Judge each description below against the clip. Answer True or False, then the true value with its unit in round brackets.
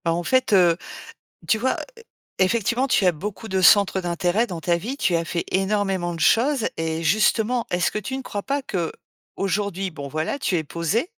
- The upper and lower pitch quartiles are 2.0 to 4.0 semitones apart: False (4.6 semitones)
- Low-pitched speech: False (195 Hz)